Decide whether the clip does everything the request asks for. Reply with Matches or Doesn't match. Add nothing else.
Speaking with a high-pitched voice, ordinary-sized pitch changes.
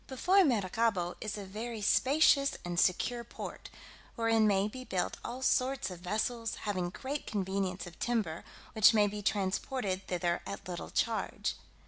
Matches